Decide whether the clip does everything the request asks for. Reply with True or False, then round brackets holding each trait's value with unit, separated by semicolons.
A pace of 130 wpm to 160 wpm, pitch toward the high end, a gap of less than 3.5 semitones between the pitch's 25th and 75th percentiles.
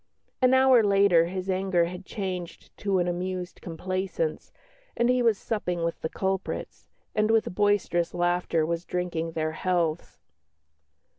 False (140 wpm; 180 Hz; 2.7 semitones)